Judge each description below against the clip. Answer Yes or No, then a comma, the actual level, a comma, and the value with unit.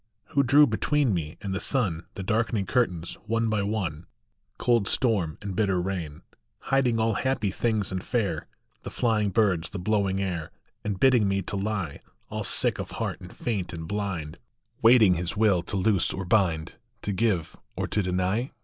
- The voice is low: Yes, low, 100 Hz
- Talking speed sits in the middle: Yes, average, 175 wpm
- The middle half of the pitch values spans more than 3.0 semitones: Yes, average, 3.7 semitones